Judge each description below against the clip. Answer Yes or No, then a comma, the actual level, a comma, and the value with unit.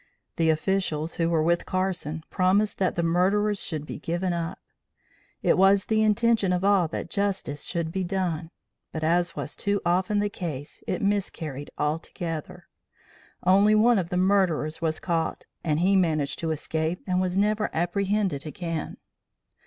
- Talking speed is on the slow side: No, average, 160 wpm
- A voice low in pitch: No, medium, 180 Hz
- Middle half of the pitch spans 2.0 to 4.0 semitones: Yes, average, 3.4 semitones